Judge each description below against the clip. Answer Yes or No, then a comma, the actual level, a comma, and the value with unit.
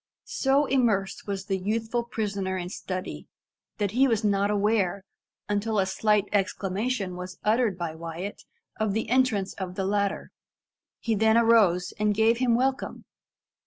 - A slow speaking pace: No, average, 150 wpm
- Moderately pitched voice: No, high, 205 Hz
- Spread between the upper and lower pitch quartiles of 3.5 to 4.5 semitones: No, average, 3.0 semitones